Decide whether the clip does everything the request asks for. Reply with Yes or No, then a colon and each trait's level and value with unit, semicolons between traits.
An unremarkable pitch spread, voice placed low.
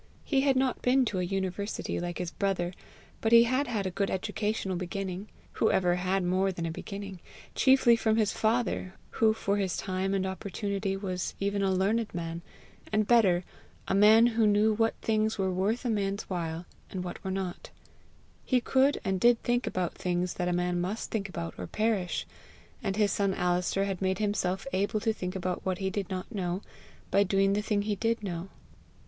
No: average, 3.0 semitones; high, 195 Hz